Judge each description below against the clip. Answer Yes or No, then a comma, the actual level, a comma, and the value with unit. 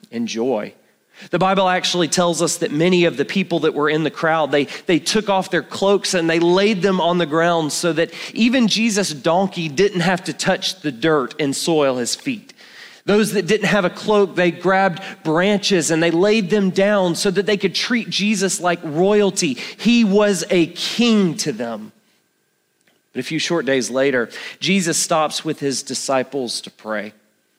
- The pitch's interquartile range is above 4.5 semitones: No, average, 4.1 semitones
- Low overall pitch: No, medium, 175 Hz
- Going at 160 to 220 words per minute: Yes, average, 185 wpm